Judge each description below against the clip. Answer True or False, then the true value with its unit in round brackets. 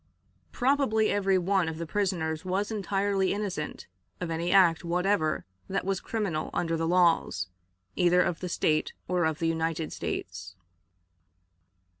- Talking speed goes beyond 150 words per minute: False (140 wpm)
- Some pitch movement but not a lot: True (3.3 semitones)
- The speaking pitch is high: False (180 Hz)